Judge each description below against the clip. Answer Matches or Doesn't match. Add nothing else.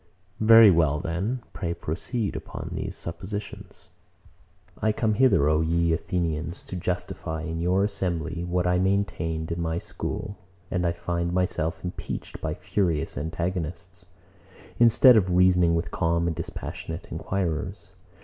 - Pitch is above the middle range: Doesn't match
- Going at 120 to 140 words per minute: Matches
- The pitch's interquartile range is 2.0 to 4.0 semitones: Matches